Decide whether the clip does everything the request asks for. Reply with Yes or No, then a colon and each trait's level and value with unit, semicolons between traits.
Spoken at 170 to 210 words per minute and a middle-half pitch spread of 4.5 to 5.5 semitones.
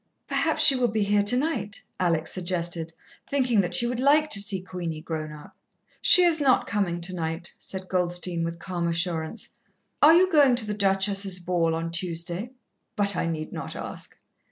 Yes: average, 175 wpm; average, 4.8 semitones